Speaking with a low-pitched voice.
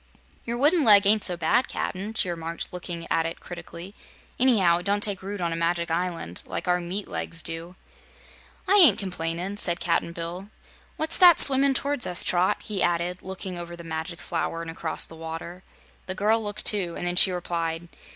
No: medium, 180 Hz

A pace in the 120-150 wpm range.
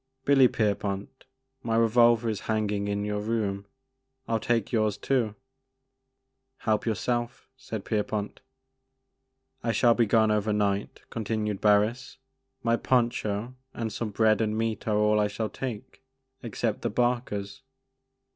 Yes: average, 145 wpm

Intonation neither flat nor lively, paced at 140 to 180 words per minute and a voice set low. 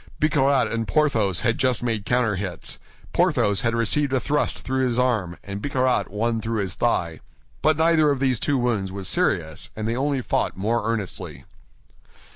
Yes: average, 4.5 semitones; average, 170 wpm; low, 115 Hz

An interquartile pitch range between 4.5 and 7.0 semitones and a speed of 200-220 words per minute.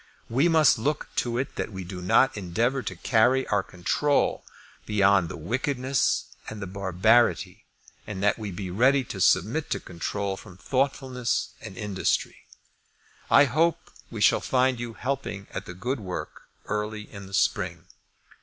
No: average, 5.3 semitones; average, 155 wpm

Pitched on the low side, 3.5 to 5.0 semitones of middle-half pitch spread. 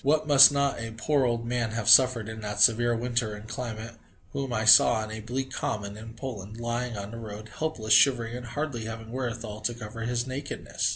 No: low, 115 Hz; narrow, 2.6 semitones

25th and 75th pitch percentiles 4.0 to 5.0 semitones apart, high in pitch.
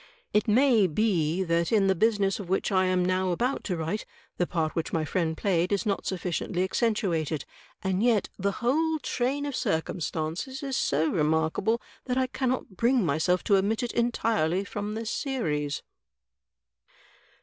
No: wide, 5.6 semitones; high, 195 Hz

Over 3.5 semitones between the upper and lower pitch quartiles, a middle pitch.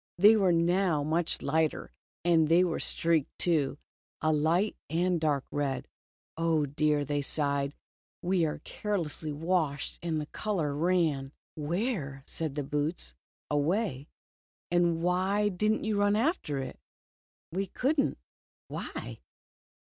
Yes: average, 3.9 semitones; medium, 165 Hz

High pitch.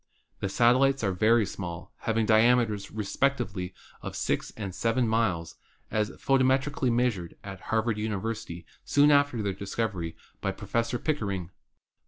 No: low, 110 Hz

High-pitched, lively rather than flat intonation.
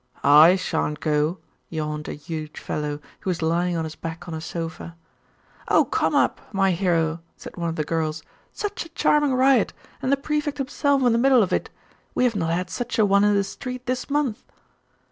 No: medium, 180 Hz; wide, 7.7 semitones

